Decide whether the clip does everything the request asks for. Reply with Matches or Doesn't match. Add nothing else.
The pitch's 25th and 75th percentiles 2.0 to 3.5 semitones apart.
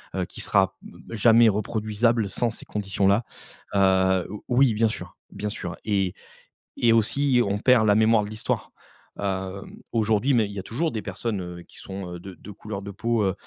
Matches